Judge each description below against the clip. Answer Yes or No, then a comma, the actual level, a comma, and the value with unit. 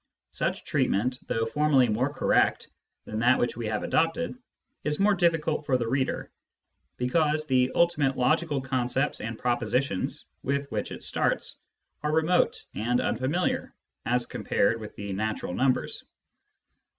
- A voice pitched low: Yes, low, 130 Hz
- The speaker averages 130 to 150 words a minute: Yes, average, 140 wpm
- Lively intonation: No, average, 4.3 semitones